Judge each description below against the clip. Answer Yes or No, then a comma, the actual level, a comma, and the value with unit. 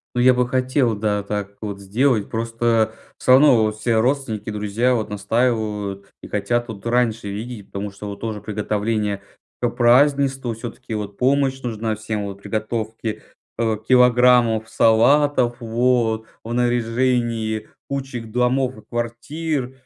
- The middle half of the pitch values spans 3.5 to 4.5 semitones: No, average, 2.7 semitones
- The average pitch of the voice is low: Yes, low, 115 Hz